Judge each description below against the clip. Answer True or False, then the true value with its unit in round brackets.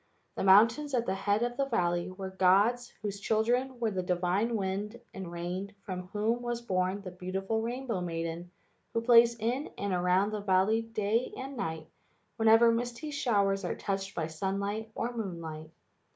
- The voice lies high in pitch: True (200 Hz)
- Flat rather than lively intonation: False (3.9 semitones)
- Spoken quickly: False (165 wpm)